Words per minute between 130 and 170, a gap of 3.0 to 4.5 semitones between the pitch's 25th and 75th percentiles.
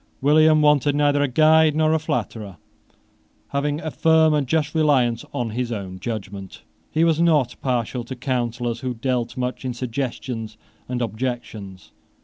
Yes: average, 150 wpm; average, 4.2 semitones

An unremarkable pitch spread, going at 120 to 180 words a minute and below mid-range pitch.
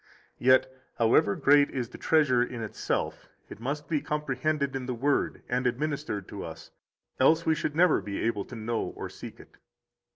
Yes: average, 3.9 semitones; average, 175 wpm; low, 130 Hz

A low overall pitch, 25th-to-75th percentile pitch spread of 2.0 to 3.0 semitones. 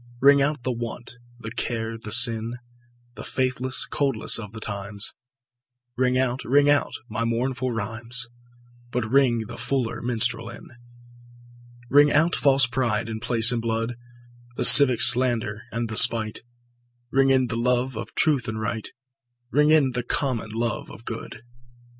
Yes: low, 120 Hz; narrow, 2.4 semitones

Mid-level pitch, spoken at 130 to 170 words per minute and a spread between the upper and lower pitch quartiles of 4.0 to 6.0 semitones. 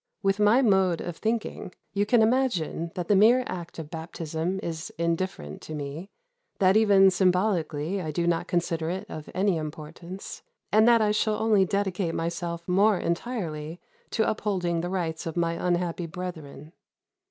No: medium, 180 Hz; average, 160 wpm; average, 3.5 semitones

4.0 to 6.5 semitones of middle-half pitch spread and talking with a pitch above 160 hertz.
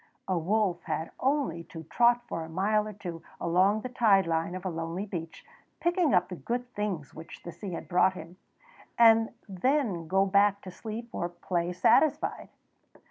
Yes: average, 4.3 semitones; high, 190 Hz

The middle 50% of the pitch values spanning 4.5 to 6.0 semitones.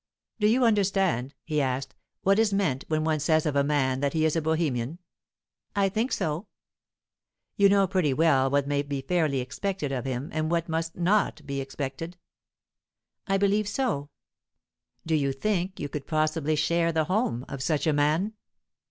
Yes: average, 5.2 semitones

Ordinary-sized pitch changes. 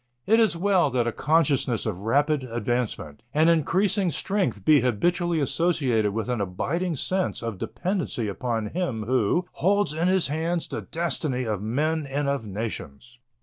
No: wide, 6.9 semitones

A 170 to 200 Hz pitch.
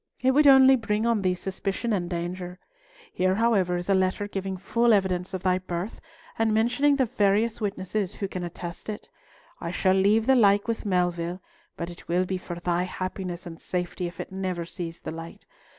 Yes: high, 190 Hz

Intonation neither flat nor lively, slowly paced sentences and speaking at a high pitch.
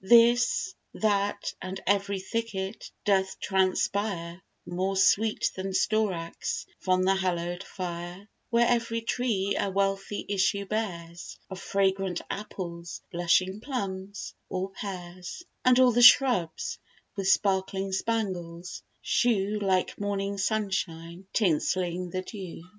No: narrow, 2.2 semitones; slow, 115 wpm; high, 195 Hz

